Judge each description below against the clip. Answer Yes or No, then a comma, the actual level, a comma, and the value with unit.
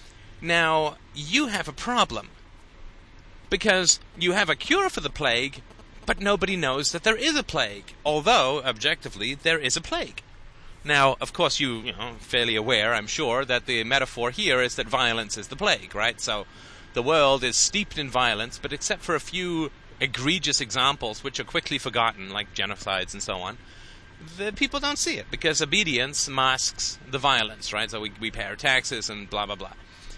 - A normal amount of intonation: No, wide, 6.7 semitones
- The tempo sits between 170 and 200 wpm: Yes, average, 185 wpm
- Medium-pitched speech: No, low, 130 Hz